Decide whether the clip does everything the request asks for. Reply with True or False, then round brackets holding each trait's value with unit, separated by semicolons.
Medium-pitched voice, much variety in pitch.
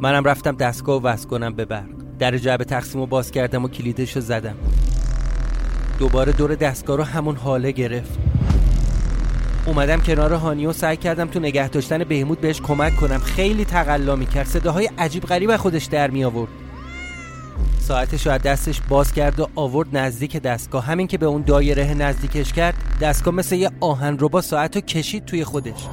False (145 Hz; 3.6 semitones)